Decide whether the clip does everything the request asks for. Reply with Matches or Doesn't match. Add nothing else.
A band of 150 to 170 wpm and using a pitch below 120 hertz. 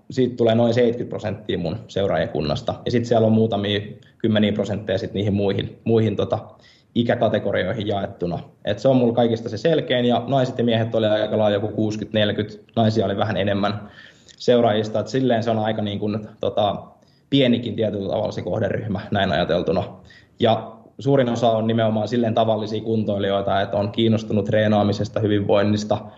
Matches